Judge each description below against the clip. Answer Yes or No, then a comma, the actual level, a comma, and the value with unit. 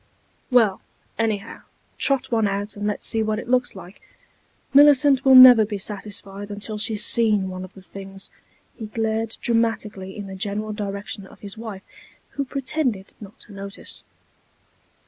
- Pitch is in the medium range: No, high, 210 Hz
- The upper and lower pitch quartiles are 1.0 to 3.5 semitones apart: Yes, narrow, 2.5 semitones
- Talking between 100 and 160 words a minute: Yes, average, 155 wpm